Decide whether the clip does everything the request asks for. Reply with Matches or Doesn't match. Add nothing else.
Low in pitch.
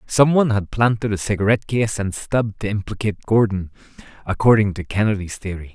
Matches